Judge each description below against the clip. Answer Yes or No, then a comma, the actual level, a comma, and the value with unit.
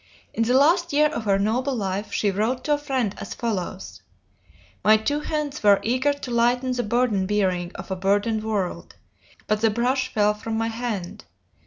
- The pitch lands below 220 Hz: No, high, 225 Hz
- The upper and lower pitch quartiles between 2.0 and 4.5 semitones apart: Yes, average, 3.9 semitones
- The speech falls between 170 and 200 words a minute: Yes, average, 185 wpm